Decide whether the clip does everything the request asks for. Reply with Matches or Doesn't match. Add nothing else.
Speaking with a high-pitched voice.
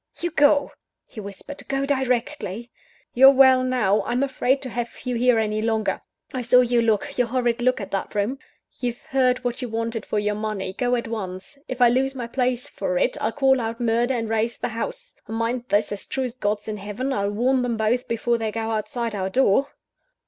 Matches